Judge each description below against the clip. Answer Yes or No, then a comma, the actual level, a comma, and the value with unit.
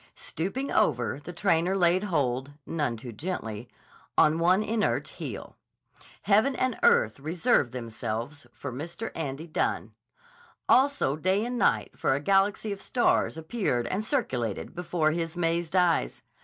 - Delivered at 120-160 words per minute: Yes, average, 140 wpm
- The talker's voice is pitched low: No, medium, 165 Hz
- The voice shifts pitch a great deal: Yes, wide, 6.6 semitones